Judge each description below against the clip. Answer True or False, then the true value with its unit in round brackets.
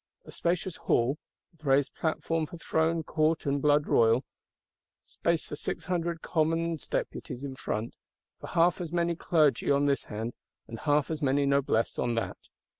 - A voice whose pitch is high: False (150 Hz)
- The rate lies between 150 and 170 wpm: True (165 wpm)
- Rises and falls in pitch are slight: False (3.3 semitones)